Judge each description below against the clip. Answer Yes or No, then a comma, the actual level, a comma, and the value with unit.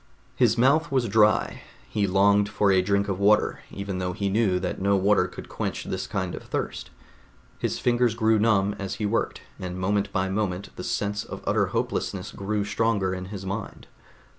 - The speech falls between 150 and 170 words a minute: No, average, 190 wpm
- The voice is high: No, low, 100 Hz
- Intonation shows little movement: Yes, narrow, 2.0 semitones